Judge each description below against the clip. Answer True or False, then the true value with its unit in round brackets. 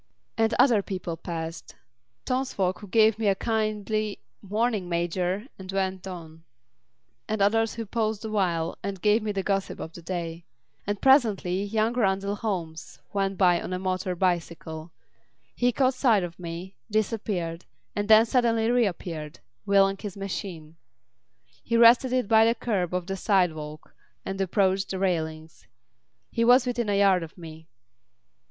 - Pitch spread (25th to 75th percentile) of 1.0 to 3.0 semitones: False (3.8 semitones)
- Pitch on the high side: True (195 Hz)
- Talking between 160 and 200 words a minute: False (150 wpm)